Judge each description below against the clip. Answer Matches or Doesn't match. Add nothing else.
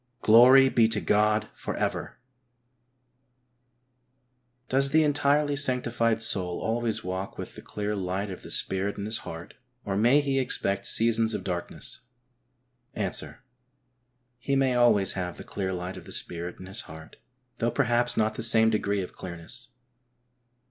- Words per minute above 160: Doesn't match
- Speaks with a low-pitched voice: Matches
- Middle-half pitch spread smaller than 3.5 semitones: Doesn't match